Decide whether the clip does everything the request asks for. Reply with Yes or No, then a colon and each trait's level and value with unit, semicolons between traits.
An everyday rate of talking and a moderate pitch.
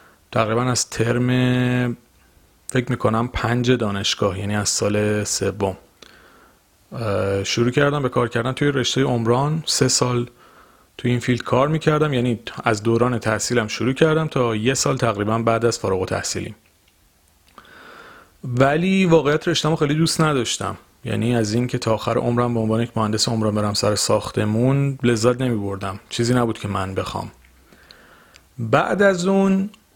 No: average, 145 wpm; low, 120 Hz